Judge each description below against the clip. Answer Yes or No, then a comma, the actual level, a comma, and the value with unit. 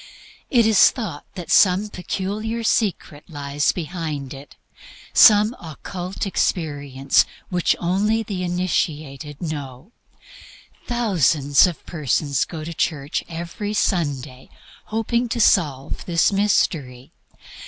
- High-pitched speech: No, medium, 170 Hz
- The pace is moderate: No, slow, 100 wpm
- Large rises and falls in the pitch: Yes, wide, 5.9 semitones